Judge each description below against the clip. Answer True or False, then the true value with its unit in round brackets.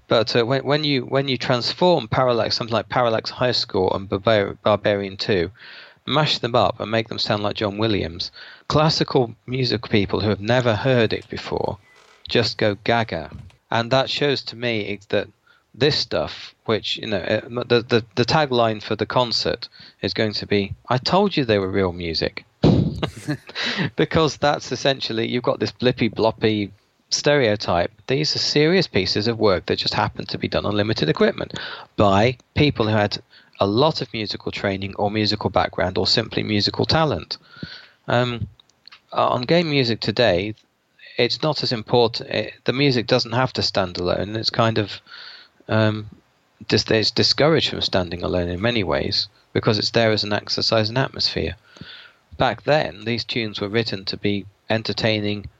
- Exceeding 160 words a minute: True (170 wpm)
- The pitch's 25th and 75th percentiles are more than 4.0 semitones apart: False (3.6 semitones)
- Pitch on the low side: True (110 Hz)